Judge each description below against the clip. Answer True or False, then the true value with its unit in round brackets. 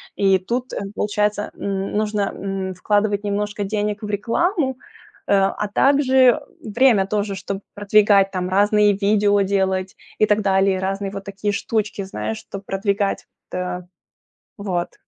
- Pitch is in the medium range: False (205 Hz)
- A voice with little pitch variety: True (1.4 semitones)